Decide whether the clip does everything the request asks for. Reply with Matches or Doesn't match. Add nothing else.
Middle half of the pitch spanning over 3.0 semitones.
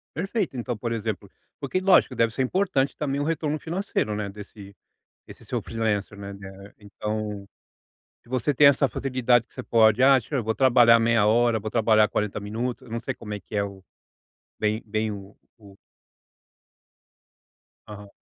Matches